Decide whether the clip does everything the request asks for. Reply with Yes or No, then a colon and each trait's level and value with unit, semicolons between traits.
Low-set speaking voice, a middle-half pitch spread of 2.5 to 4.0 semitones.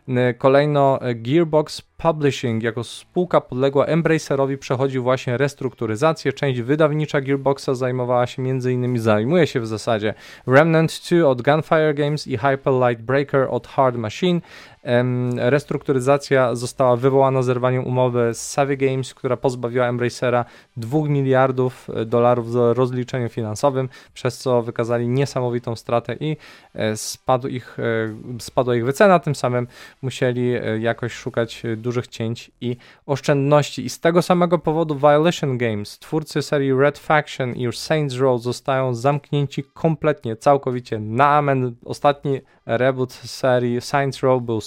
Yes: low, 130 Hz; average, 2.9 semitones